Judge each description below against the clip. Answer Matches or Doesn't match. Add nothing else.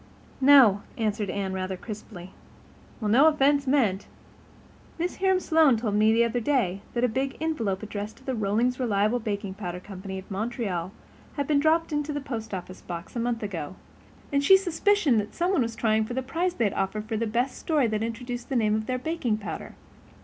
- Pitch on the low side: Doesn't match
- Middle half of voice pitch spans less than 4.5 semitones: Doesn't match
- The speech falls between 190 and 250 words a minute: Matches